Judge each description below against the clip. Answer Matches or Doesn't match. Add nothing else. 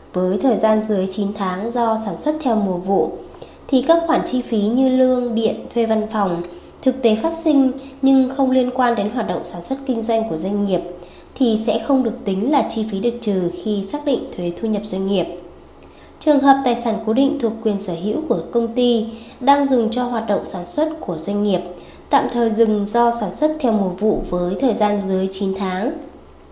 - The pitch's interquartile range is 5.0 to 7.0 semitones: Doesn't match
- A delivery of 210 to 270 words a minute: Matches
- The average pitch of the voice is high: Matches